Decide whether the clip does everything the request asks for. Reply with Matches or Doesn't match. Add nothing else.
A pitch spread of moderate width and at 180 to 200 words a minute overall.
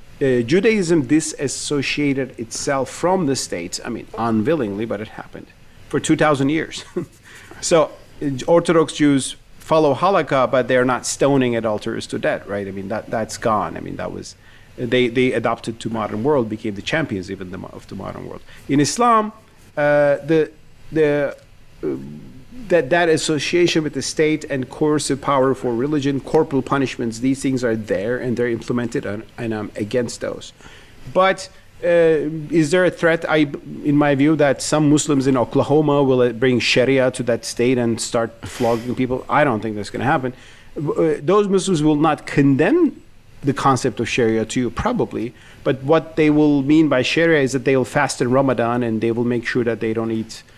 Matches